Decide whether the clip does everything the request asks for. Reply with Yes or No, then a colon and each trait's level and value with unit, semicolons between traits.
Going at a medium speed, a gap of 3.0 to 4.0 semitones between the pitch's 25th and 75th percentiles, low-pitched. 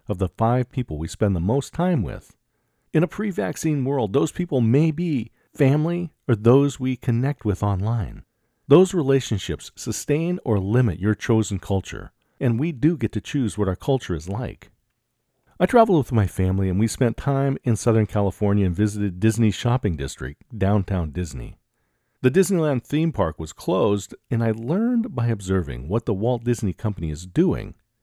No: average, 175 wpm; wide, 5.5 semitones; low, 115 Hz